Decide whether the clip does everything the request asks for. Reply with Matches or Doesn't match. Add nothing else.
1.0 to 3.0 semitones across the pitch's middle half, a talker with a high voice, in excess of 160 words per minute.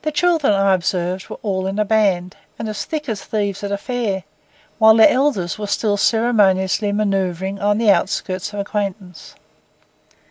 Matches